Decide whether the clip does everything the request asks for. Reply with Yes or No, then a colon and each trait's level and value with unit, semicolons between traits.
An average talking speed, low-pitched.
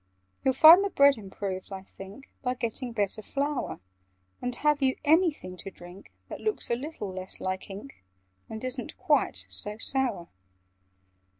No: average, 155 wpm; high, 240 Hz